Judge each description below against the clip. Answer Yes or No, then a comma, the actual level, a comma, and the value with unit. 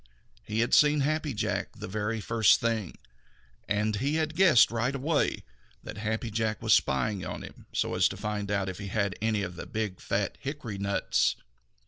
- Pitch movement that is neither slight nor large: Yes, average, 4.1 semitones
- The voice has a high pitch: No, low, 110 Hz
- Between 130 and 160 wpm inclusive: No, average, 185 wpm